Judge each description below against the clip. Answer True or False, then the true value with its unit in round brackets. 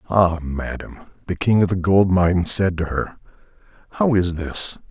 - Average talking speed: True (170 wpm)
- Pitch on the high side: False (90 Hz)